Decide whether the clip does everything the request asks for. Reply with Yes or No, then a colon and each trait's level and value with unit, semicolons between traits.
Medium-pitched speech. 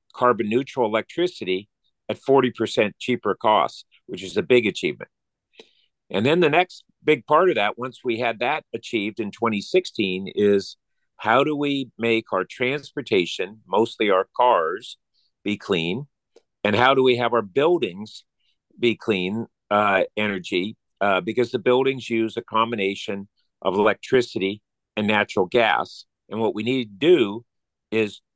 No: low, 115 Hz